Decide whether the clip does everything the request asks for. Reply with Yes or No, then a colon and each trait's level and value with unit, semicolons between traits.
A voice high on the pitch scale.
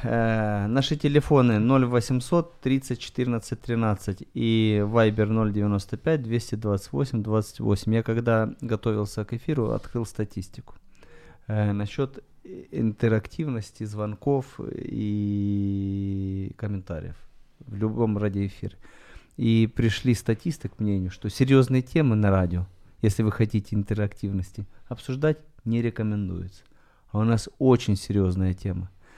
No: low, 110 Hz